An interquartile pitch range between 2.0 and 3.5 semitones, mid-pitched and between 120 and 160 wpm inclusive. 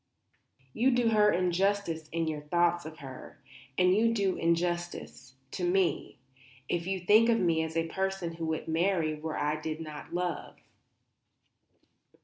Yes: average, 3.1 semitones; medium, 175 Hz; average, 150 wpm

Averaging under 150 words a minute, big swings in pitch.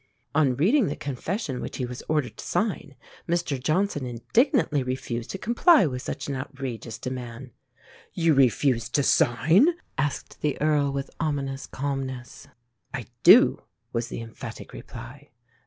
No: average, 140 wpm; average, 3.6 semitones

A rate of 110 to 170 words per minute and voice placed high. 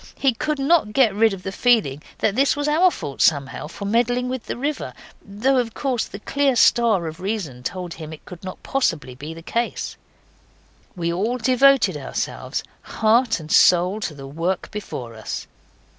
No: average, 180 wpm; high, 210 Hz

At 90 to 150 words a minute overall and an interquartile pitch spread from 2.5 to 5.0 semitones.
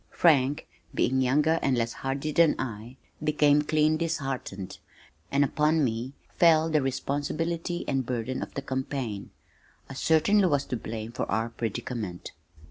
Yes: average, 140 wpm; average, 4.2 semitones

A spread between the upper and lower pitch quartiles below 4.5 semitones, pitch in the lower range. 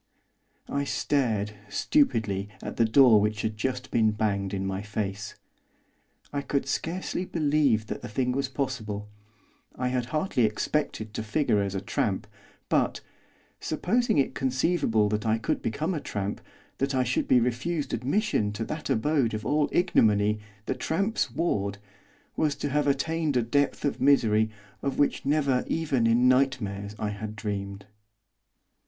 No: average, 5.2 semitones; low, 125 Hz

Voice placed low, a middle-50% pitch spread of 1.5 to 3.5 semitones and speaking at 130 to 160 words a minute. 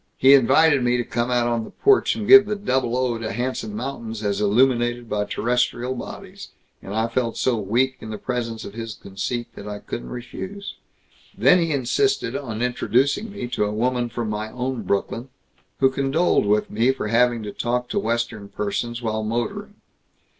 No: low, 120 Hz; average, 3.1 semitones; average, 185 wpm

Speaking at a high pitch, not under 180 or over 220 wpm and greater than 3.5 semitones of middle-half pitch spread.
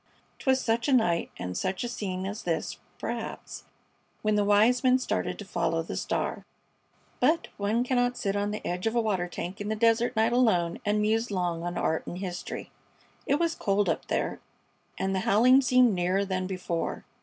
Yes: high, 205 Hz; average, 190 wpm; average, 4.6 semitones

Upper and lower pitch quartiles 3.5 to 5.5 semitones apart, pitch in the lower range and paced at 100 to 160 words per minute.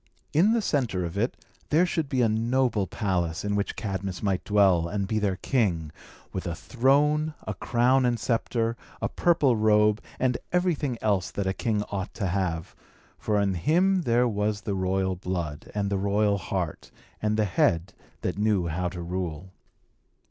No: average, 4.5 semitones; low, 105 Hz; average, 175 wpm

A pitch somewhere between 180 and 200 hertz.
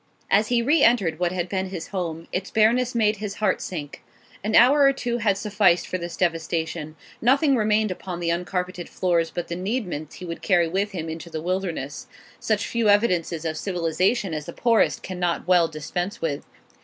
Yes: medium, 185 Hz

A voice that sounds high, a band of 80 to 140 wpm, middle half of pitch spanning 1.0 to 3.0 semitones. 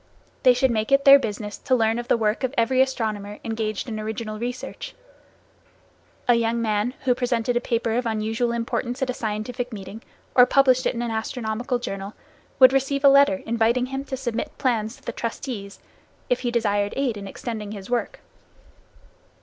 No: high, 235 Hz; average, 180 wpm; narrow, 2.6 semitones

